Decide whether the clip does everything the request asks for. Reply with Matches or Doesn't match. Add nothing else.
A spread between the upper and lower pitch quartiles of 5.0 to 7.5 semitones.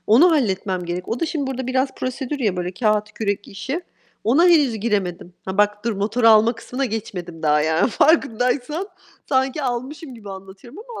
Matches